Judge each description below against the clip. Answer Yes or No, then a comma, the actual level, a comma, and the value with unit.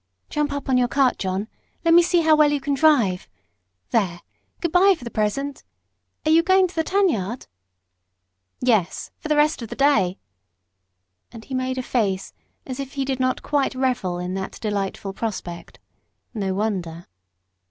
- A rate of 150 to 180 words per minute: Yes, average, 175 wpm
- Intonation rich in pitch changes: Yes, wide, 6.9 semitones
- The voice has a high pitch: Yes, very high, 255 Hz